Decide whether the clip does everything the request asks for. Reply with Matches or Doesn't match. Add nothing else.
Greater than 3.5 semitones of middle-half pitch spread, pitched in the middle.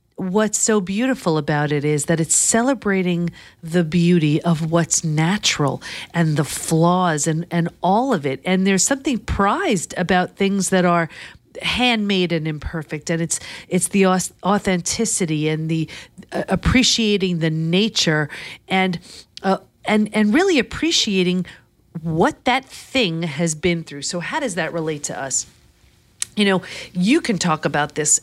Matches